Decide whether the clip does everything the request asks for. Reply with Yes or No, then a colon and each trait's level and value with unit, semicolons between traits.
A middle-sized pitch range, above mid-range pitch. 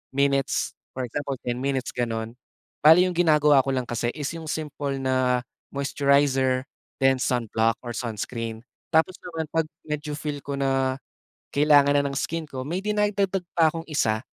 No: average, 3.5 semitones; medium, 140 Hz